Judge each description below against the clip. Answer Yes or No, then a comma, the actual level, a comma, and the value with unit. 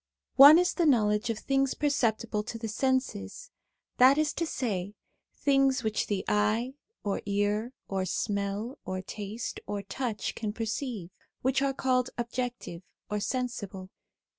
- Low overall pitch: No, high, 230 Hz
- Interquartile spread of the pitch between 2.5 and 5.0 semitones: Yes, average, 4.2 semitones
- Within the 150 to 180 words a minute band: No, average, 140 wpm